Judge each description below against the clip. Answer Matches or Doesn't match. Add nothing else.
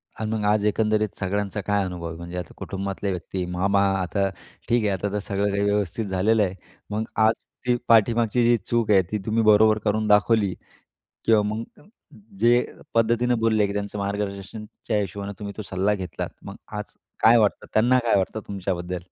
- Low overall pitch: Matches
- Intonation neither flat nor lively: Doesn't match